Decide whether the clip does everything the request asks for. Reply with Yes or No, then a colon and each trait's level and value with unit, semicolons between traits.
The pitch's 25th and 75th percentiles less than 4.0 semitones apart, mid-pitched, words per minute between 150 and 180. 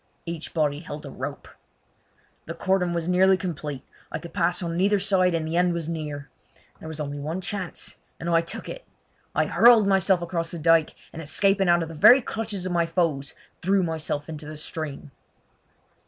No: average, 3.1 semitones; medium, 170 Hz; average, 190 wpm